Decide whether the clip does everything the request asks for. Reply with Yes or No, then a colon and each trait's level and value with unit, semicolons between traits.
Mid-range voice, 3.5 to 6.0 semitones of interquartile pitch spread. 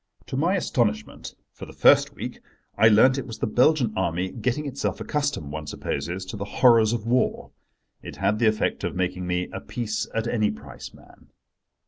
No: low, 110 Hz; average, 5.1 semitones